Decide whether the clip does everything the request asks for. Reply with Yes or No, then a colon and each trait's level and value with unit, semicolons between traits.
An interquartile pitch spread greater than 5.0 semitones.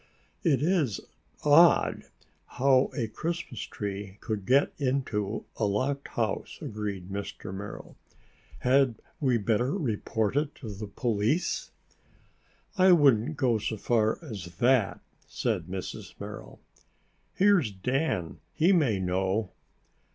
Yes: wide, 5.6 semitones